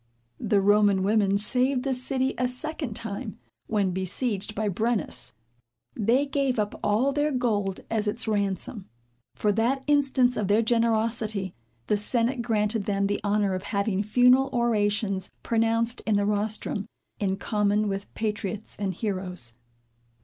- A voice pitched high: Yes, high, 215 Hz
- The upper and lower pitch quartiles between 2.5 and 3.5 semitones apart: Yes, average, 3.1 semitones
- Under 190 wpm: Yes, average, 140 wpm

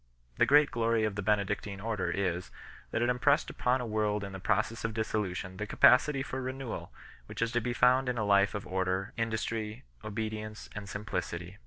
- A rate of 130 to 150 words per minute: No, average, 190 wpm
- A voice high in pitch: No, low, 110 Hz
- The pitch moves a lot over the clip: No, average, 3.3 semitones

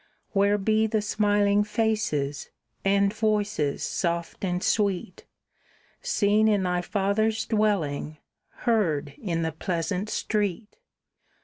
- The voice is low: No, high, 200 Hz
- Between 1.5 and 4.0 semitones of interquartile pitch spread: Yes, average, 3.3 semitones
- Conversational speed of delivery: No, slow, 105 wpm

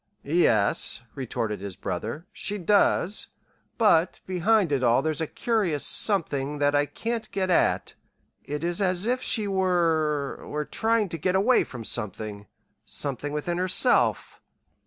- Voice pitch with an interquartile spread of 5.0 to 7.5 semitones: Yes, wide, 5.5 semitones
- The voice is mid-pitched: Yes, medium, 165 Hz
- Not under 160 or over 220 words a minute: No, average, 140 wpm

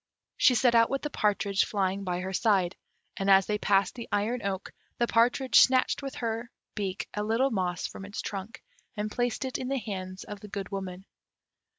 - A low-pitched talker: No, high, 210 Hz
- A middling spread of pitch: Yes, average, 3.5 semitones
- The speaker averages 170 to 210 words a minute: Yes, average, 200 wpm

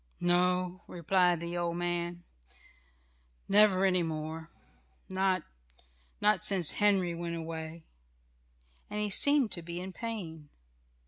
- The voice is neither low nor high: Yes, medium, 175 Hz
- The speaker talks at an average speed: No, slow, 115 wpm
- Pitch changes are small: Yes, narrow, 2.3 semitones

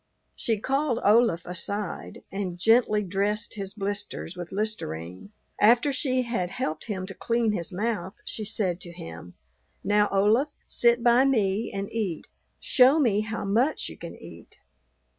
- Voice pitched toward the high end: Yes, high, 210 Hz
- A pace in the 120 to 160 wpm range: Yes, average, 150 wpm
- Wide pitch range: No, average, 3.7 semitones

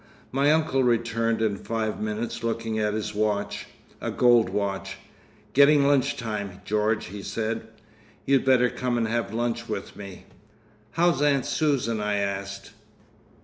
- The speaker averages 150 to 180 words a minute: No, slow, 135 wpm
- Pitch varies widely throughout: No, average, 3.1 semitones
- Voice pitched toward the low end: Yes, low, 115 Hz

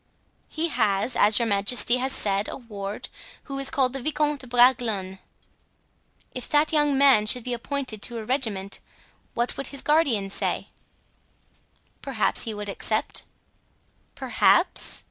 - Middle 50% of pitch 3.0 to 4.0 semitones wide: No, average, 4.5 semitones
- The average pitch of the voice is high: Yes, high, 245 Hz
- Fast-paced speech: No, average, 145 wpm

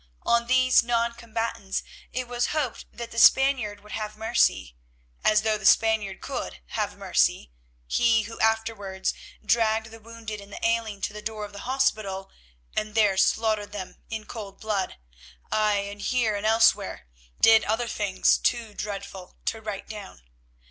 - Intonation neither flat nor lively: No, narrow, 2.1 semitones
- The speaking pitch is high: Yes, high, 215 Hz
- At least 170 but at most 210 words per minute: No, average, 155 wpm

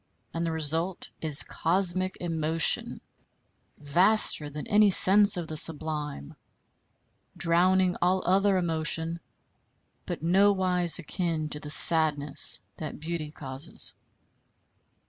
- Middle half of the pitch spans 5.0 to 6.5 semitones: No, average, 3.2 semitones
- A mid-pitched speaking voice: Yes, medium, 165 Hz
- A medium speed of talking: No, slow, 105 wpm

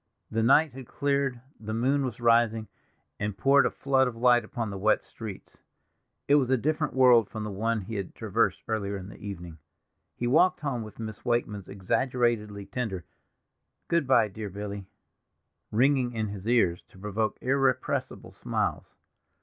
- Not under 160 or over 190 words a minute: Yes, average, 165 wpm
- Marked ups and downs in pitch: No, average, 3.9 semitones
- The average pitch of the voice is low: Yes, low, 115 Hz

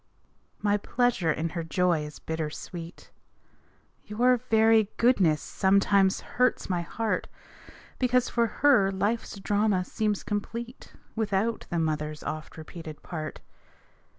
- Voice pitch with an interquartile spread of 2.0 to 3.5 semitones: No, average, 5.3 semitones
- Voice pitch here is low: No, high, 200 Hz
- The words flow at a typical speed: No, slow, 120 wpm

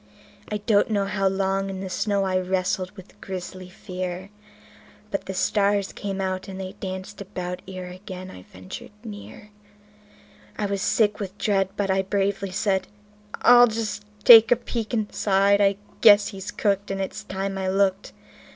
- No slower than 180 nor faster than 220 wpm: No, average, 170 wpm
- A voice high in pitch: Yes, high, 195 Hz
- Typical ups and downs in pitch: No, narrow, 1.5 semitones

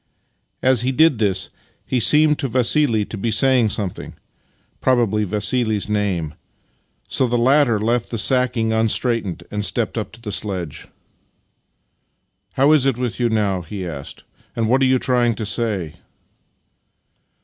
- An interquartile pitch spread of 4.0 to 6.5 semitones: No, average, 3.6 semitones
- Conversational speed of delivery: Yes, average, 165 wpm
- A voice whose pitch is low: Yes, low, 115 Hz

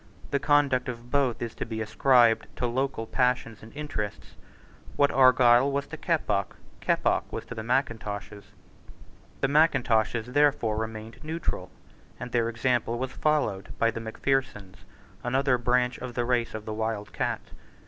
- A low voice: Yes, low, 120 Hz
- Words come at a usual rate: Yes, average, 150 wpm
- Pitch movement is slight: No, average, 3.3 semitones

